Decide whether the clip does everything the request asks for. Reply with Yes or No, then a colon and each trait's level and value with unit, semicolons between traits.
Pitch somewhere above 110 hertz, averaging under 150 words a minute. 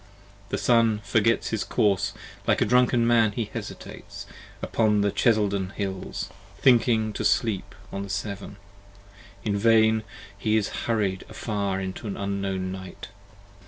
No: low, 105 Hz; average, 140 wpm